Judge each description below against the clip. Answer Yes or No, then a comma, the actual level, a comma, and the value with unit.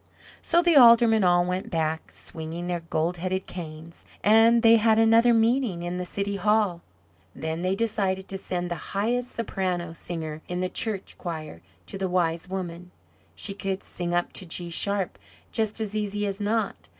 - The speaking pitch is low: No, high, 190 Hz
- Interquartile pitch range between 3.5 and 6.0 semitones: Yes, average, 3.9 semitones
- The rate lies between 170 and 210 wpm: Yes, average, 175 wpm